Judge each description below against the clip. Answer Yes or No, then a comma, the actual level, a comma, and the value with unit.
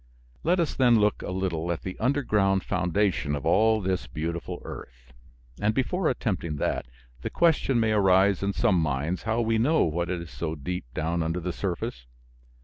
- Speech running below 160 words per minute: No, average, 175 wpm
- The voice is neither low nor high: No, very low, 95 Hz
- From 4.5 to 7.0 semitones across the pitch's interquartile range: Yes, average, 5.0 semitones